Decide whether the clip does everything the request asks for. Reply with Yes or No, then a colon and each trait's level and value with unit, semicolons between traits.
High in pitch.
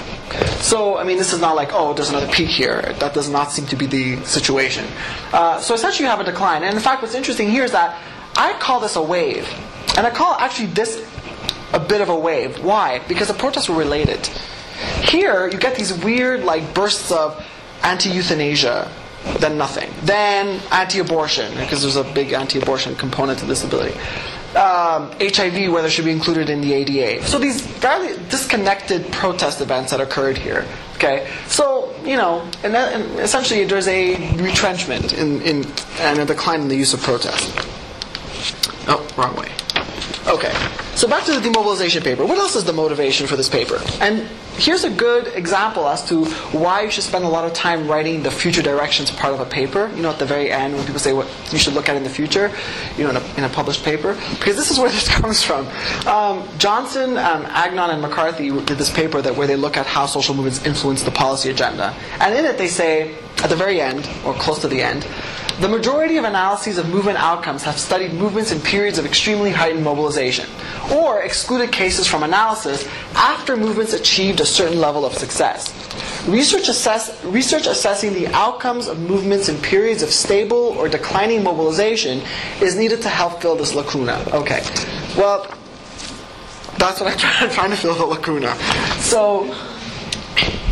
No: medium, 175 Hz